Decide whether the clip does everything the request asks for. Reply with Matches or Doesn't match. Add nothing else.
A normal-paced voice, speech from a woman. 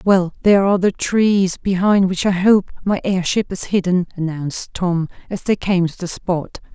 Matches